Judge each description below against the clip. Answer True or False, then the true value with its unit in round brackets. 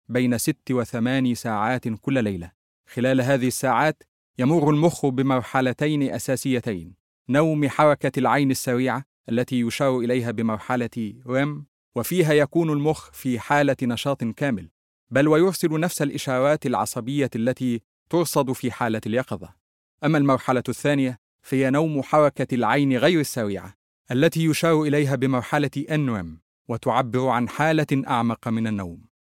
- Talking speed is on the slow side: True (125 wpm)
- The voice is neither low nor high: False (130 Hz)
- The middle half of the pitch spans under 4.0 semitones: True (3.4 semitones)